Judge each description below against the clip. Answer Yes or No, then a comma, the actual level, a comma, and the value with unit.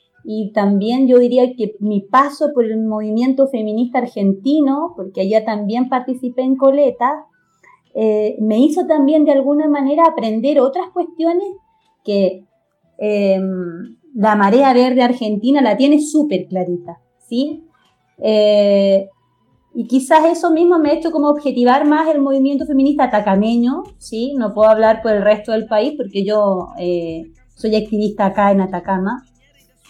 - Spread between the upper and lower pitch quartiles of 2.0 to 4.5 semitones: No, wide, 5.4 semitones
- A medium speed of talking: Yes, average, 140 wpm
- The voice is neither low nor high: No, high, 240 Hz